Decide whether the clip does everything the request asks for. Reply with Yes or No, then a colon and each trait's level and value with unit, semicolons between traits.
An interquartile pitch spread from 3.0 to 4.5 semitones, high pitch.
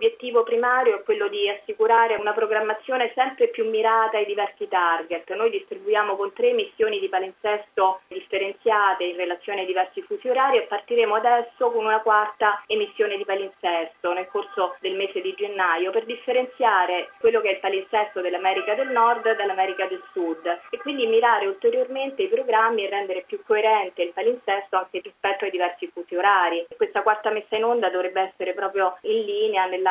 No: average, 5.3 semitones; high, 215 Hz